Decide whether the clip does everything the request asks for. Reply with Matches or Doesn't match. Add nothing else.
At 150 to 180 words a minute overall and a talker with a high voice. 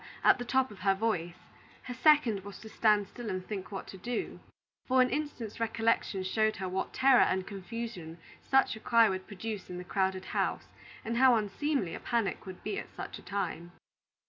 Doesn't match